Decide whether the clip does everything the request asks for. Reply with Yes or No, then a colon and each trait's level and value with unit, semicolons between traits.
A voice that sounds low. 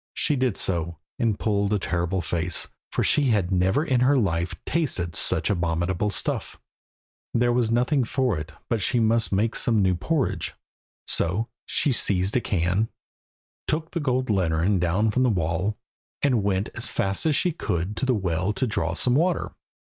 Yes: low, 105 Hz